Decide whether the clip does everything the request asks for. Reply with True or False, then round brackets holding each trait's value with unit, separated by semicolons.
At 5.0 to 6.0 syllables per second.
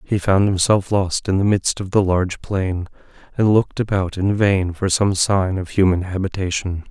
False (4.7 syllables/s)